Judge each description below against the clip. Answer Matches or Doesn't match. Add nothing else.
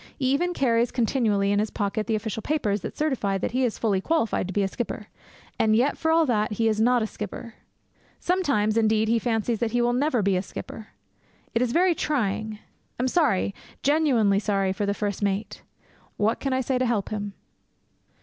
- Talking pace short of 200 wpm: Doesn't match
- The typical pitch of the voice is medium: Doesn't match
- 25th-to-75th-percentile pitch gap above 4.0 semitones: Doesn't match